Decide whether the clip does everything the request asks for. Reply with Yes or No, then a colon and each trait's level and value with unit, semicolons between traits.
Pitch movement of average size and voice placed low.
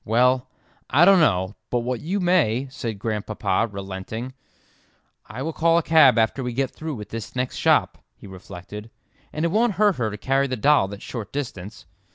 No: wide, 6.2 semitones; low, 125 Hz